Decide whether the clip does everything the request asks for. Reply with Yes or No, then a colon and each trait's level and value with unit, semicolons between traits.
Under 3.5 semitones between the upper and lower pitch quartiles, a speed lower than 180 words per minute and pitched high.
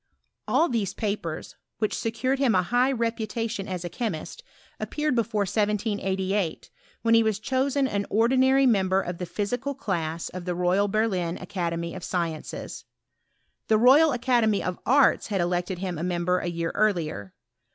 No: average, 4.7 semitones; average, 155 wpm; high, 205 Hz